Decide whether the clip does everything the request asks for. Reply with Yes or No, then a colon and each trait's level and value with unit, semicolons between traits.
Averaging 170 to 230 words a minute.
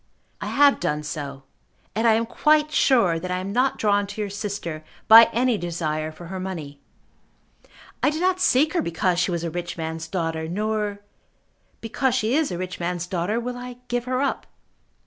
Yes: average, 190 wpm